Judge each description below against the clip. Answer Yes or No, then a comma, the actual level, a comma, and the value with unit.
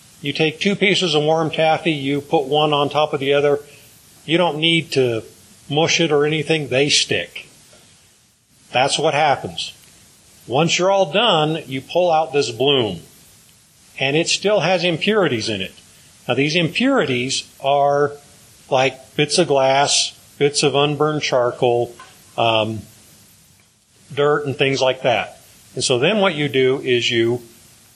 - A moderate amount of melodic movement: Yes, average, 3.6 semitones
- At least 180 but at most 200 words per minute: No, average, 150 wpm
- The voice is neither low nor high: Yes, medium, 145 Hz